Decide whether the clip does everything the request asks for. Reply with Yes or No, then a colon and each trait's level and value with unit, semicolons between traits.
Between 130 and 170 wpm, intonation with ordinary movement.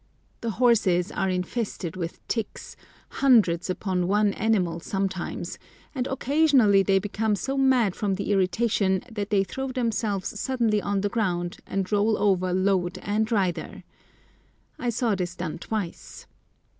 Yes: average, 140 wpm; average, 3.4 semitones